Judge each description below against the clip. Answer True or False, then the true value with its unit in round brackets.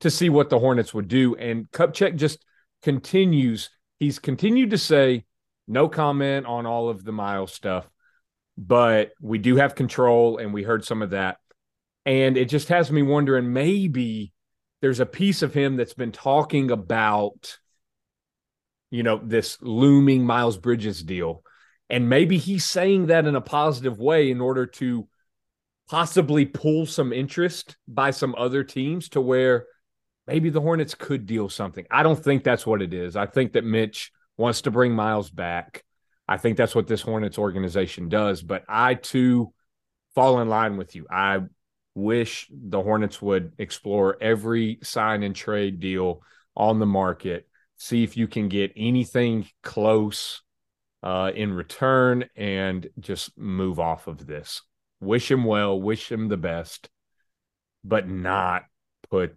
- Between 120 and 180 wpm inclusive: True (160 wpm)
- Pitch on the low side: True (115 Hz)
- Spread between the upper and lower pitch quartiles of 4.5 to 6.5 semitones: True (5.0 semitones)